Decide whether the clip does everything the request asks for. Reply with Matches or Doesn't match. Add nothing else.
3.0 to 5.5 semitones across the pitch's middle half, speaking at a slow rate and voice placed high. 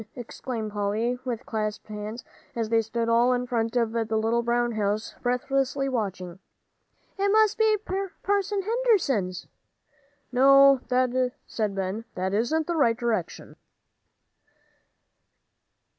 Matches